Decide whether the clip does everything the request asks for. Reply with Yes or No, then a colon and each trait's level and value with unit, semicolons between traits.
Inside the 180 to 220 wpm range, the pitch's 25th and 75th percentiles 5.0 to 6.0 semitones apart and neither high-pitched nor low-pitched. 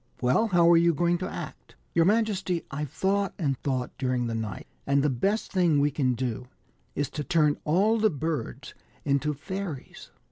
Yes: average, 190 wpm; average, 5.3 semitones; medium, 150 Hz